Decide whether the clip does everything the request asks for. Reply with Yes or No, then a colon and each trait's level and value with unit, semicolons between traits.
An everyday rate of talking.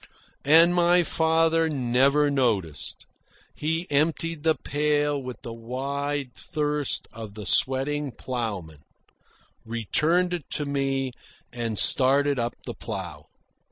No: slow, 115 wpm